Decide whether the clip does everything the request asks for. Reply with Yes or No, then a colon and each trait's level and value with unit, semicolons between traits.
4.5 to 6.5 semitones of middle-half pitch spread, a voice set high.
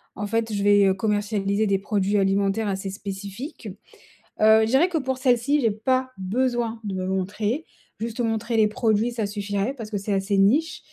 No: average, 2.9 semitones; high, 215 Hz